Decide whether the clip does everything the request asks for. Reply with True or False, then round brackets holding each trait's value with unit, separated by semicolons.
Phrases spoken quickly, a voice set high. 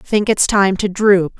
True (215 wpm; 195 Hz)